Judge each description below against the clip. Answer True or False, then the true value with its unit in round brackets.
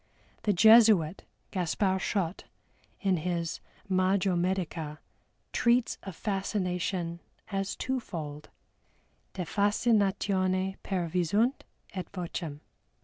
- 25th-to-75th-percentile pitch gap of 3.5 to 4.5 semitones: False (2.7 semitones)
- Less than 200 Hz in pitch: True (185 Hz)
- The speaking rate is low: True (85 wpm)